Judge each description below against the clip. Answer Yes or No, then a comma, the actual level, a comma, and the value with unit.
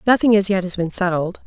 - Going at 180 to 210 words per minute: No, fast, 245 wpm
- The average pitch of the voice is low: No, high, 190 Hz